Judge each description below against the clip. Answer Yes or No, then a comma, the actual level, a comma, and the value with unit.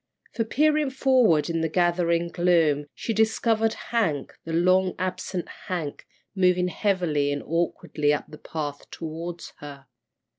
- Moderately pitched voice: Yes, medium, 175 Hz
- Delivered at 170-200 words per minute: No, slow, 135 wpm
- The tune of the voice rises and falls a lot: No, average, 4.3 semitones